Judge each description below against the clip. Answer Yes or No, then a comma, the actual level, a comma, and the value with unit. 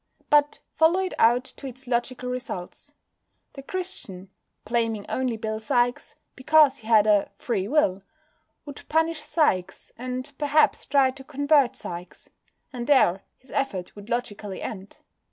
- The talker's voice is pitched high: Yes, very high, 250 Hz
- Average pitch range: Yes, average, 4.9 semitones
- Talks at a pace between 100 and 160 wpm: Yes, average, 140 wpm